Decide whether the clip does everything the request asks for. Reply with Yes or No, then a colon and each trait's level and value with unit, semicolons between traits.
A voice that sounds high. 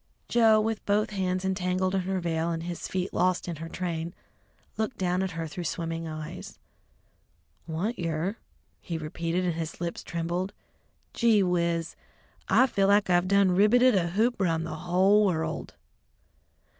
No: medium, 180 Hz